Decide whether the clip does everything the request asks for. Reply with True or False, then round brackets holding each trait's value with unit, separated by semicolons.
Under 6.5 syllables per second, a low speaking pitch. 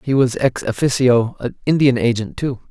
True (5.0 syllables/s; 125 Hz)